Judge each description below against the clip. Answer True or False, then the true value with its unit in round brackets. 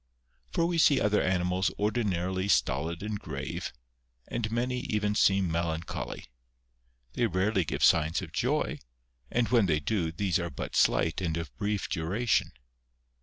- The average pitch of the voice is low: True (95 Hz)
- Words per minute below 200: True (145 wpm)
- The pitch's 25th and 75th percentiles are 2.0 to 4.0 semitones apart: False (4.4 semitones)